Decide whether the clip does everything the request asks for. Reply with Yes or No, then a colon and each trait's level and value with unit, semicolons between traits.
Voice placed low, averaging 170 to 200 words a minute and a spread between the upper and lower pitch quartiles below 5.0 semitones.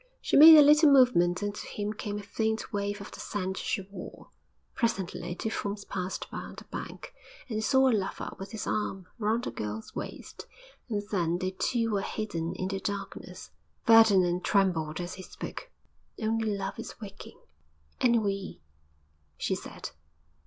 No: high, 205 Hz; average, 175 wpm; average, 2.9 semitones